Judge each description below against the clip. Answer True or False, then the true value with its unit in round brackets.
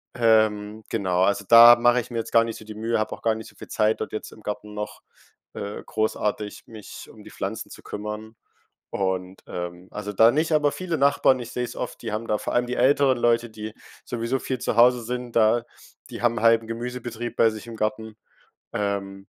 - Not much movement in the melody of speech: True (2.2 semitones)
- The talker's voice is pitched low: True (110 Hz)